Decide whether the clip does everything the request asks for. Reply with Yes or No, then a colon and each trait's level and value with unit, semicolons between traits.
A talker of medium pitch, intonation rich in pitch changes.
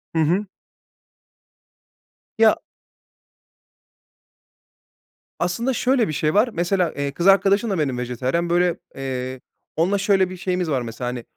Yes: medium, 175 Hz; wide, 6.4 semitones